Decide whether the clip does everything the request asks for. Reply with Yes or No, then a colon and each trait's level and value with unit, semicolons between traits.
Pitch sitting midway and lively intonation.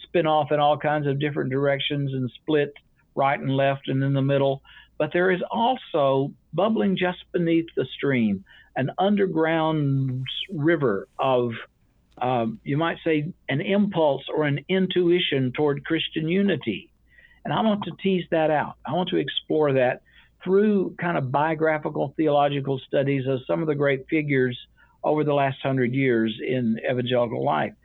No: medium, 145 Hz; average, 3.8 semitones